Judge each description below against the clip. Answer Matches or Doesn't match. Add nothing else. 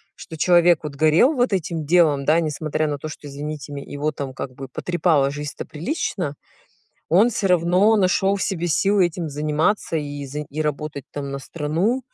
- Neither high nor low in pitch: Matches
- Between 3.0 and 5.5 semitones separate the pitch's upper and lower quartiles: Matches